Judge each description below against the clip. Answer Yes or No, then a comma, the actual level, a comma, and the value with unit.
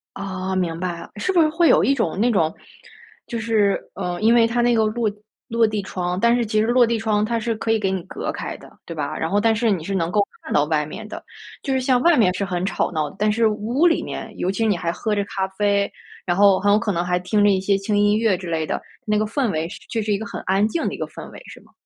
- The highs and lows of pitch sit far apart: No, average, 3.5 semitones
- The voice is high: Yes, high, 205 Hz